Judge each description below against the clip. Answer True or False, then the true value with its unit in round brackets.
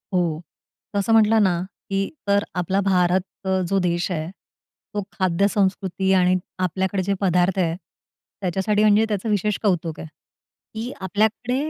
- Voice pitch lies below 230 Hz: True (190 Hz)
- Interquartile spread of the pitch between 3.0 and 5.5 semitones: False (2.4 semitones)